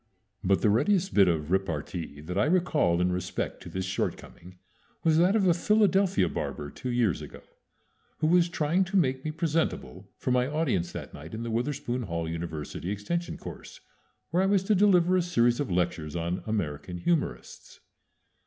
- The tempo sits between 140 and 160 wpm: No, average, 175 wpm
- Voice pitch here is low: Yes, low, 120 Hz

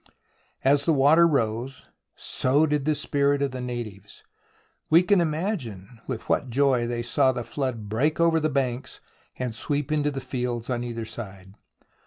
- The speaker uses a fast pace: No, average, 165 wpm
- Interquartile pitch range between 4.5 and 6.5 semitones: No, average, 3.7 semitones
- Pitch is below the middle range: Yes, low, 130 Hz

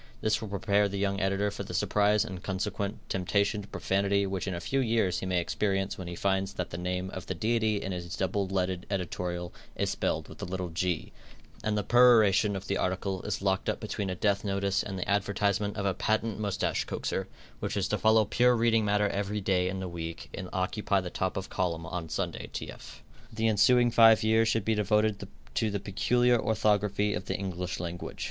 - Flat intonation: Yes, narrow, 2.2 semitones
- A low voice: Yes, low, 100 Hz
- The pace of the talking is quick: Yes, fast, 210 wpm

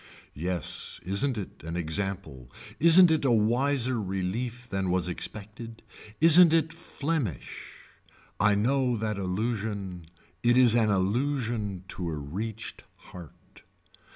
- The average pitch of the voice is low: Yes, low, 110 Hz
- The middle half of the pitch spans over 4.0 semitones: Yes, average, 5.2 semitones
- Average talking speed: No, slow, 120 wpm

